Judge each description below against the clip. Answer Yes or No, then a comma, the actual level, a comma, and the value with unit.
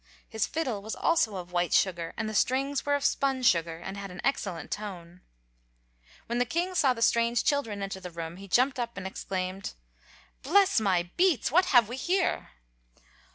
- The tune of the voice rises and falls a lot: Yes, wide, 6.6 semitones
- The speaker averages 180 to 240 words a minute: Yes, average, 185 wpm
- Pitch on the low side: No, high, 220 Hz